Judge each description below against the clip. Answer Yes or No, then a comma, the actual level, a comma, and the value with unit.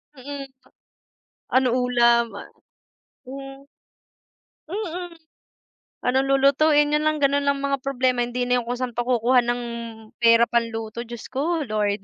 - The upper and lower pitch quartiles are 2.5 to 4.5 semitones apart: Yes, average, 2.9 semitones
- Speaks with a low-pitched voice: No, very high, 255 Hz